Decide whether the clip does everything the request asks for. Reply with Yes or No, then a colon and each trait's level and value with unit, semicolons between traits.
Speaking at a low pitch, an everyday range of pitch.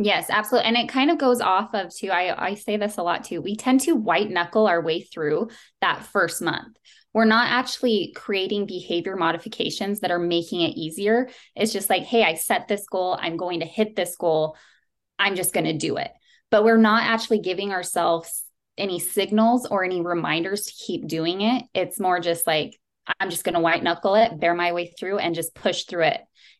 No: high, 195 Hz; average, 4.2 semitones